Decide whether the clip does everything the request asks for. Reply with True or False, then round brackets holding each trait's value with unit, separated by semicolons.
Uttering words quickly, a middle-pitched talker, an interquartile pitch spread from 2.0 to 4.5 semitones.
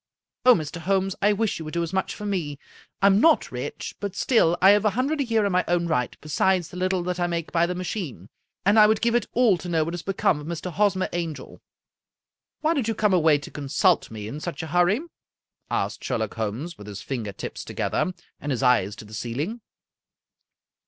False (225 wpm; 175 Hz; 5.2 semitones)